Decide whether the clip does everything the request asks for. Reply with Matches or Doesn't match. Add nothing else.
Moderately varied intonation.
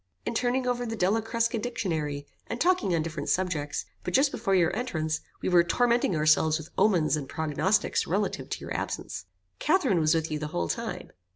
Doesn't match